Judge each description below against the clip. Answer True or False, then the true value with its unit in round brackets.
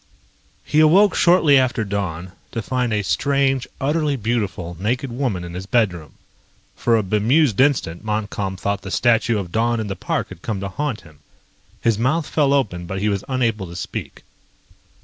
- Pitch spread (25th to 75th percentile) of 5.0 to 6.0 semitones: True (5.5 semitones)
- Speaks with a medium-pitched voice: False (110 Hz)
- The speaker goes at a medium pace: True (175 wpm)